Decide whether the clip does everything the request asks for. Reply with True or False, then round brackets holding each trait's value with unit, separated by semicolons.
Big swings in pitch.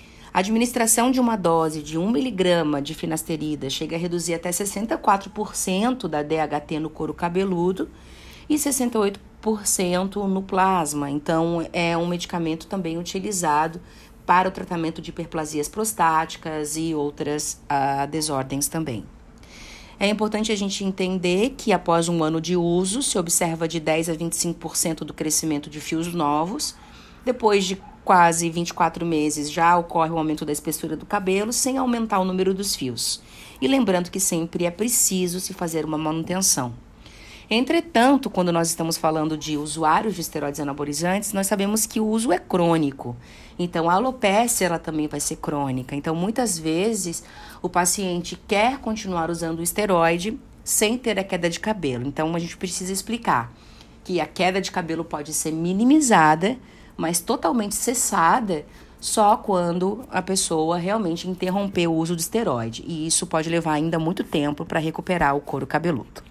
False (4.0 semitones)